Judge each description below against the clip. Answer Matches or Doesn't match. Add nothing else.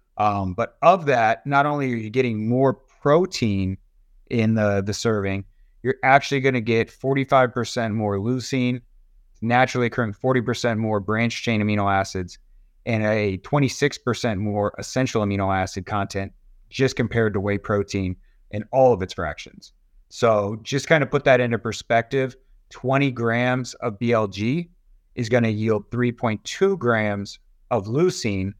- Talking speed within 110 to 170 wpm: Matches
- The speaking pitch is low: Matches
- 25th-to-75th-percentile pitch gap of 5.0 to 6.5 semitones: Doesn't match